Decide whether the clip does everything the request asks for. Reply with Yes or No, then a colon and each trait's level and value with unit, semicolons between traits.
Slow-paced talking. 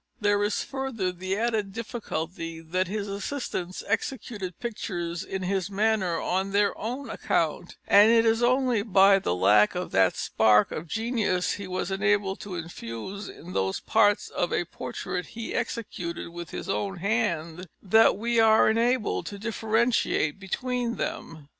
No: average, 155 wpm